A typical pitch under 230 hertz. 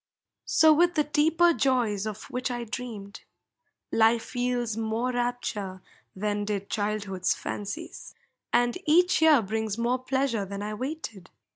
No: high, 235 Hz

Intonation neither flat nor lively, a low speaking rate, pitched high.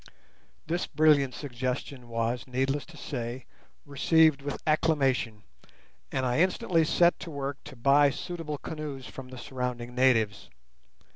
No: average, 3.4 semitones; slow, 130 wpm; low, 135 Hz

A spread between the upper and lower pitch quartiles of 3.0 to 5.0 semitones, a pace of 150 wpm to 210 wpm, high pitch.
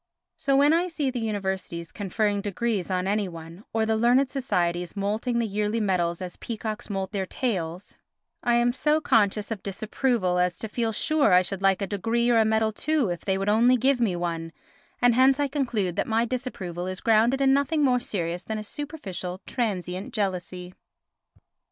Yes: average, 4.7 semitones; average, 190 wpm; high, 215 Hz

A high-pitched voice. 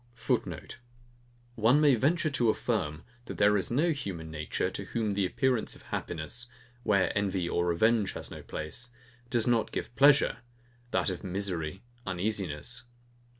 No: low, 105 Hz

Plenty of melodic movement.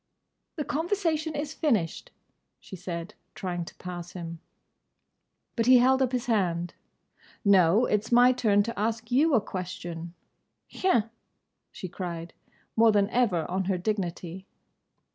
Yes: wide, 5.8 semitones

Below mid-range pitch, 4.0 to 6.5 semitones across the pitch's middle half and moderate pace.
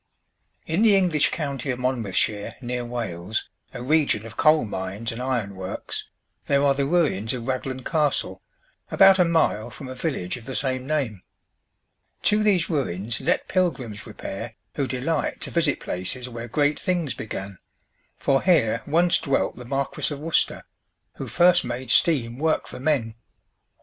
Yes: low, 130 Hz; average, 5.3 semitones; average, 160 wpm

